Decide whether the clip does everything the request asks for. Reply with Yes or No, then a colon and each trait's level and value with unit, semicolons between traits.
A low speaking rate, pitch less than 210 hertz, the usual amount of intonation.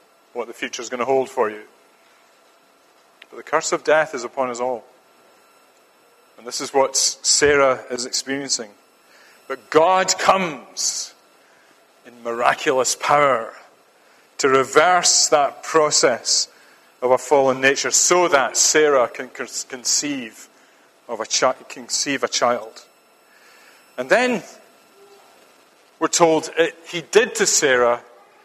Yes: slow, 125 wpm; medium, 140 Hz; average, 4.6 semitones